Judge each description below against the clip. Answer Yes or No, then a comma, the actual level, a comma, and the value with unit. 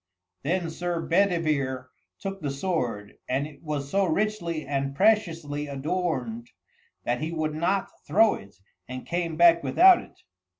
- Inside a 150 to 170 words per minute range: No, average, 140 wpm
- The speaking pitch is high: No, medium, 160 Hz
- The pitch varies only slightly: No, average, 4.4 semitones